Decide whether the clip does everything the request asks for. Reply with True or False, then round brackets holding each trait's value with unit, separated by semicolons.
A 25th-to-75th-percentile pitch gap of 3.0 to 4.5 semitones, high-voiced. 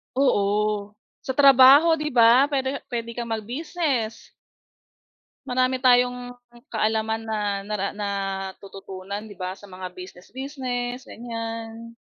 True (4.0 semitones; 230 Hz)